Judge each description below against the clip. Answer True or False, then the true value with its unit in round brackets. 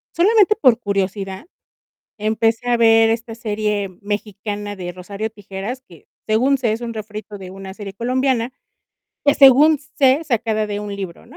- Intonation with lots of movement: False (3.2 semitones)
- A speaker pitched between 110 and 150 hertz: False (220 Hz)